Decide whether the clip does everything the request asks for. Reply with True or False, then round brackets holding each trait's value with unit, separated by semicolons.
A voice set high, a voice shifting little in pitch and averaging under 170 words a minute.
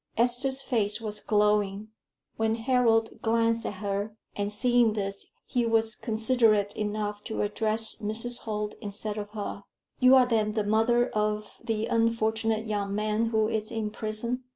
True (220 Hz; 1.5 semitones; 155 wpm)